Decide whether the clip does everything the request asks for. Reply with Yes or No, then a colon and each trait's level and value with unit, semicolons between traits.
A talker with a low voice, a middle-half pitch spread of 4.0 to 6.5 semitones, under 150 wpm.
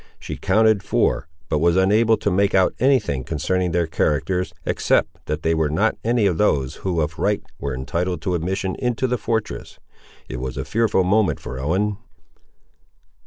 No: very low, 90 Hz; average, 5.2 semitones; average, 175 wpm